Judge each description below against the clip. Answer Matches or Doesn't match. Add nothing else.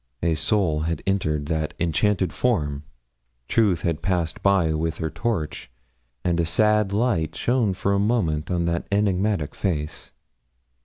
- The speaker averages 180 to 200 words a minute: Doesn't match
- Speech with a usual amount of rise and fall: Matches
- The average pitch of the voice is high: Doesn't match